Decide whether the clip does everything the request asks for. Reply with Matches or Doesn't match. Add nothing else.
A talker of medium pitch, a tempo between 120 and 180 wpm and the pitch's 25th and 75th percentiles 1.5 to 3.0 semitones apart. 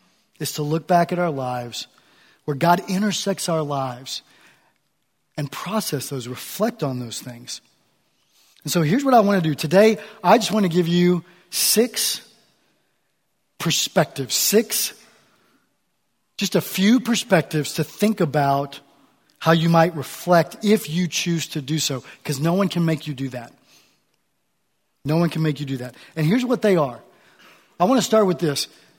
Doesn't match